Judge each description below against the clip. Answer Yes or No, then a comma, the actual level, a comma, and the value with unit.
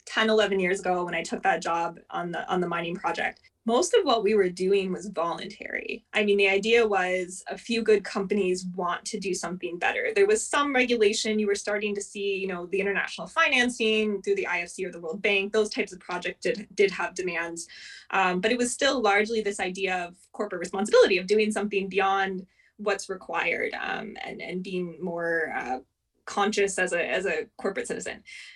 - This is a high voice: Yes, high, 195 Hz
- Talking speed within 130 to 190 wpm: No, average, 200 wpm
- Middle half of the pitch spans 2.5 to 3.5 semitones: Yes, average, 3.0 semitones